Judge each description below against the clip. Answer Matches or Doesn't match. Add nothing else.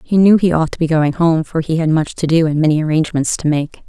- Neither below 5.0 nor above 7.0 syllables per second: Matches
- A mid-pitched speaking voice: Matches